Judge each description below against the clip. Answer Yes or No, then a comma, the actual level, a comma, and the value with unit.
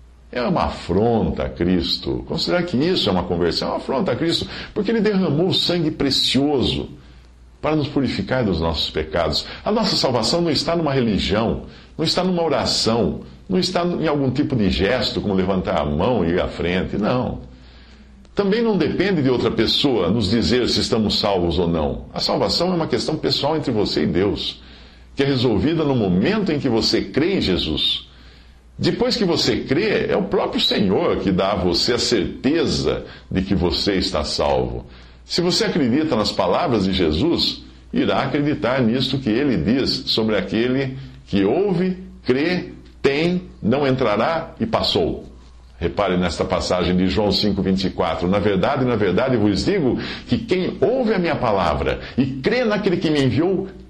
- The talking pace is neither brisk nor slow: Yes, average, 175 wpm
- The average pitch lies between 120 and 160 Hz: No, low, 110 Hz